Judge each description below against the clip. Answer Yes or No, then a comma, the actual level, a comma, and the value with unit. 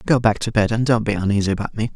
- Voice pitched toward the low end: Yes, low, 110 Hz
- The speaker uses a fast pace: Yes, fast, 310 wpm